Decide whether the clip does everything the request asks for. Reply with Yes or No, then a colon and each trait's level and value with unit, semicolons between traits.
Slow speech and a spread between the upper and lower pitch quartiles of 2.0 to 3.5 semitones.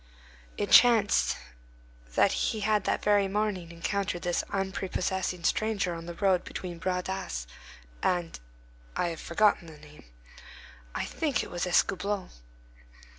Yes: slow, 125 wpm; average, 3.1 semitones